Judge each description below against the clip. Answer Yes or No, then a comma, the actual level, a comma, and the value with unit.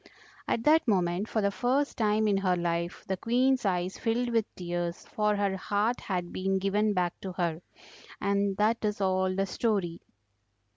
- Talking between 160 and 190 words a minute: Yes, average, 175 wpm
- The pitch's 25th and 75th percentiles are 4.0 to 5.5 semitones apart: No, average, 3.1 semitones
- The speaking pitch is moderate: No, high, 200 Hz